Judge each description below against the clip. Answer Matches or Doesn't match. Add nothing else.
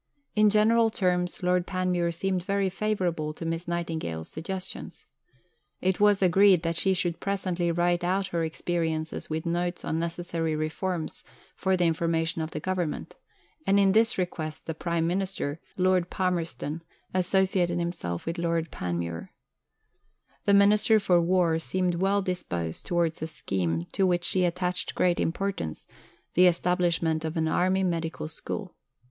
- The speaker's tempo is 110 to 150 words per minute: Matches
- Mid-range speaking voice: Matches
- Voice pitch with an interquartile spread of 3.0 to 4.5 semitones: Doesn't match